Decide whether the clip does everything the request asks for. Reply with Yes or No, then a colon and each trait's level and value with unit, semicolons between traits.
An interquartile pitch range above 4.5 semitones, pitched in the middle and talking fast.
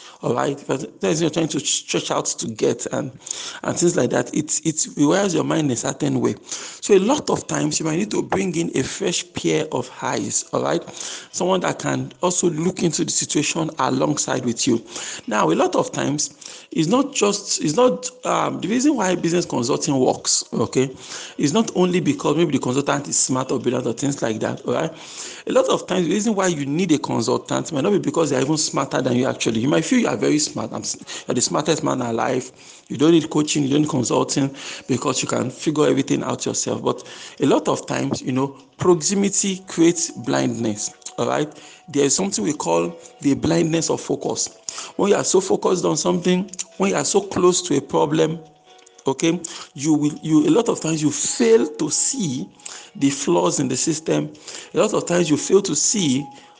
Yes: average, 4.9 semitones; medium, 160 Hz; fast, 210 wpm